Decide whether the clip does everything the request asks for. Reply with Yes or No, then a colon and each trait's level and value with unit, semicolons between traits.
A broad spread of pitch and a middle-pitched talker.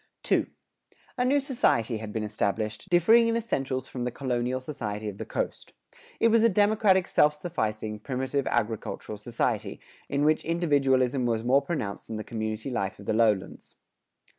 No: wide, 7.3 semitones; low, 130 Hz